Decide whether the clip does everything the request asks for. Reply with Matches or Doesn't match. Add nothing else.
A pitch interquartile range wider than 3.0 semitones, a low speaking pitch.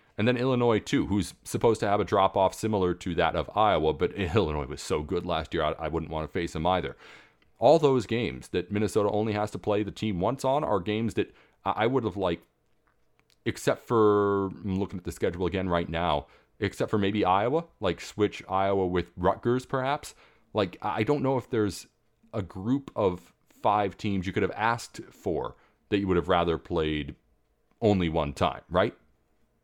Matches